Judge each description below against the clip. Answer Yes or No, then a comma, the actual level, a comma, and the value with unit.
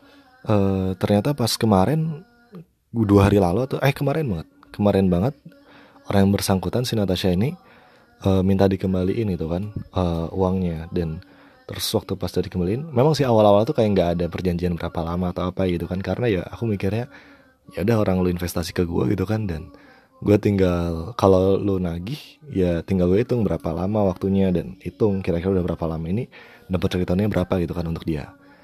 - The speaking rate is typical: No, fast, 180 wpm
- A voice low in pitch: Yes, very low, 95 Hz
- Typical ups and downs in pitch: Yes, average, 3.7 semitones